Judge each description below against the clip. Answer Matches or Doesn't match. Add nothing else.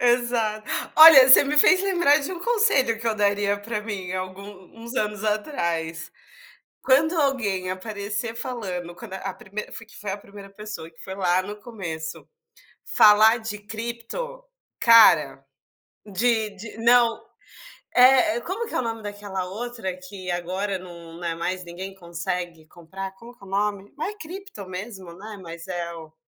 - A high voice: Matches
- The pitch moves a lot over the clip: Doesn't match